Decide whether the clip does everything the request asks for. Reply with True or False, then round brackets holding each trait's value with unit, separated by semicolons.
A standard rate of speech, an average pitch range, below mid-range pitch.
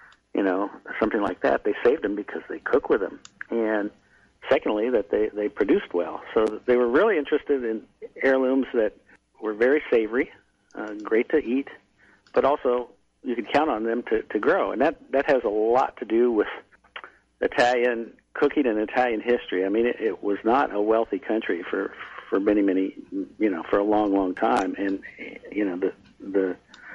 False (185 wpm; 6.2 semitones; 120 Hz)